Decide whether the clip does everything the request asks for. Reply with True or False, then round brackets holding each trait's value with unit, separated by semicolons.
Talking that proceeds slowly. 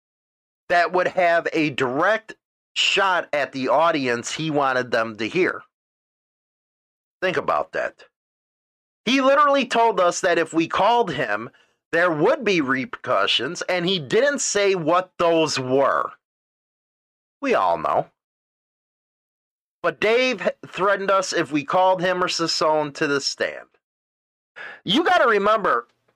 True (130 wpm)